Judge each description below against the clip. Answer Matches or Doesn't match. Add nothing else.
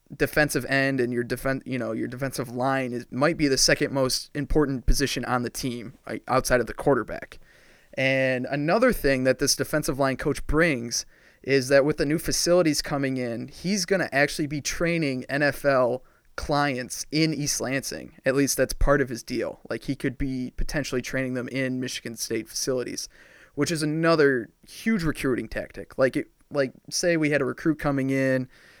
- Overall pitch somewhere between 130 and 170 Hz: Matches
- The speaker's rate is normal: Matches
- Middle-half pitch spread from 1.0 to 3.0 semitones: Matches